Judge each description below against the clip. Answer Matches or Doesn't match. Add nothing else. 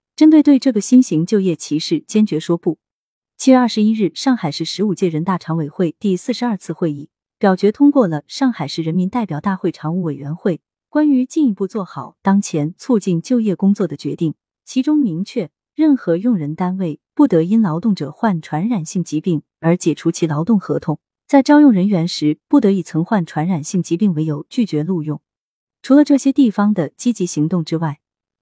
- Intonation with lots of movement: Matches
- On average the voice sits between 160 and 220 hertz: Matches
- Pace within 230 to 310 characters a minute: Matches